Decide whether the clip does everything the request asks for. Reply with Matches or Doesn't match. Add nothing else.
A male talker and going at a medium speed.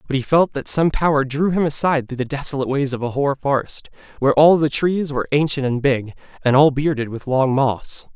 Doesn't match